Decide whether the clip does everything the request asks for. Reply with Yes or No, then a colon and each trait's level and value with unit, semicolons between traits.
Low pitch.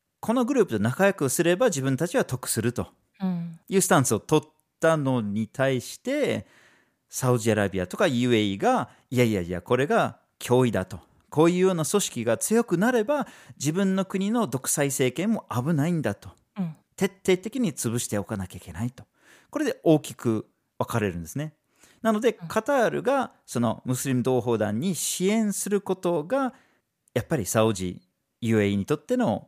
No: medium, 145 Hz